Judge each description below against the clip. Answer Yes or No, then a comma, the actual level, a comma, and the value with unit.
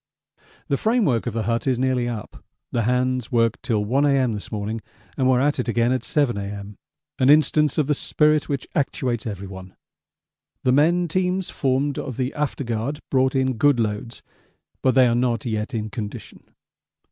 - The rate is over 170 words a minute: Yes, average, 180 wpm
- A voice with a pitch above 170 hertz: No, low, 125 Hz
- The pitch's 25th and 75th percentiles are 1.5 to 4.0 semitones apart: Yes, average, 3.7 semitones